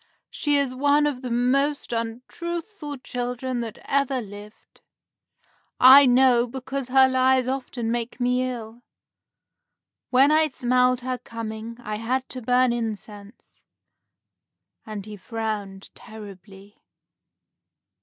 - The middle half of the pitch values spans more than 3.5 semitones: No, average, 2.7 semitones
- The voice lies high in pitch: Yes, very high, 250 Hz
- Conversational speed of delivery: No, slow, 115 wpm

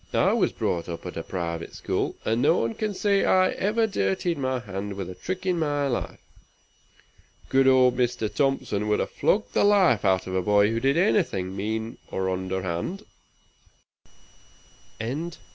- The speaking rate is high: No, average, 165 wpm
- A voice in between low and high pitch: No, low, 115 Hz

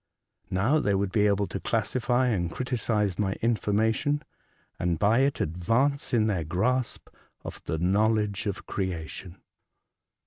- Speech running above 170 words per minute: No, average, 140 wpm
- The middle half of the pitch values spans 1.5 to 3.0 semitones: No, average, 4.1 semitones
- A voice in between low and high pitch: No, low, 105 Hz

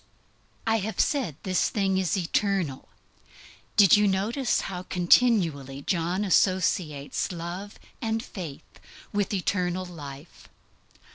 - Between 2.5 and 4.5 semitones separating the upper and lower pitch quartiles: Yes, average, 3.3 semitones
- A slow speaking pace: Yes, slow, 115 wpm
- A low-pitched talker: No, medium, 185 Hz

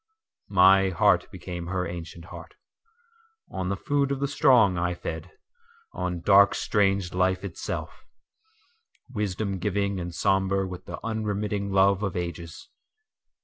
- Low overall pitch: Yes, very low, 95 Hz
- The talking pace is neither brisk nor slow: No, slow, 120 wpm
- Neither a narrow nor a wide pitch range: Yes, average, 3.0 semitones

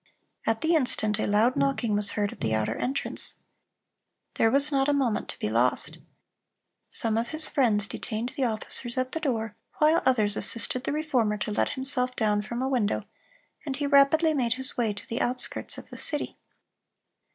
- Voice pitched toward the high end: Yes, high, 245 Hz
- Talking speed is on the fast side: No, average, 185 wpm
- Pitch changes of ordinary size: Yes, average, 4.4 semitones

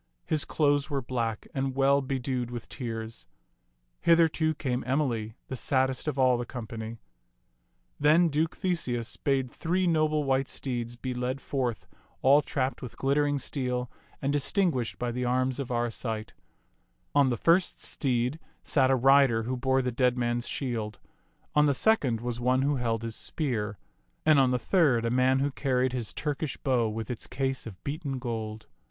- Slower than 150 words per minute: No, average, 170 wpm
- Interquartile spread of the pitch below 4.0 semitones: Yes, average, 2.9 semitones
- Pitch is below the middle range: Yes, low, 130 Hz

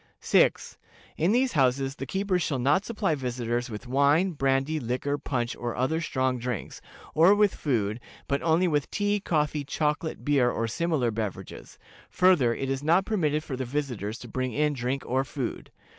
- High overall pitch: No, medium, 140 Hz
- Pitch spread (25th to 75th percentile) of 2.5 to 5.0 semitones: Yes, average, 4.4 semitones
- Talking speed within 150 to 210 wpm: Yes, average, 175 wpm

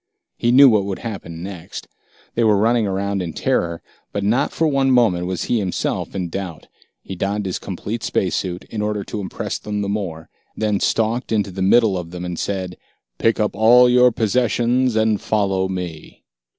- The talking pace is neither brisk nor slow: Yes, average, 190 wpm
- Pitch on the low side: Yes, low, 100 Hz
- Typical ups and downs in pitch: Yes, average, 3.5 semitones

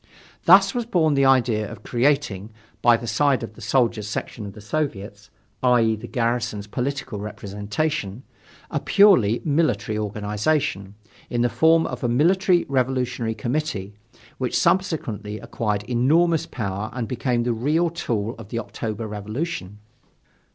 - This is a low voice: Yes, low, 120 Hz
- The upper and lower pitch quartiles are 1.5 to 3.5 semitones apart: No, wide, 5.6 semitones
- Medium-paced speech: Yes, average, 145 wpm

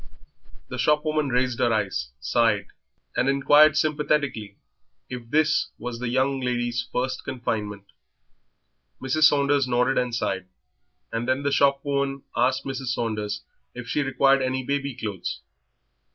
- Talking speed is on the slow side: Yes, slow, 130 wpm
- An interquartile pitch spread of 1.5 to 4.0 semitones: Yes, average, 2.8 semitones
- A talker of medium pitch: No, low, 130 Hz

